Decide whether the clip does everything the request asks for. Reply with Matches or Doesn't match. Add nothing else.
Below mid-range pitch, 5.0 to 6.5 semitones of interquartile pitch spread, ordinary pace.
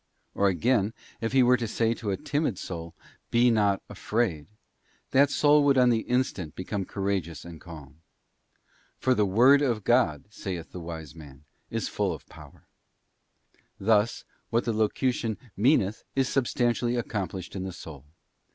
Matches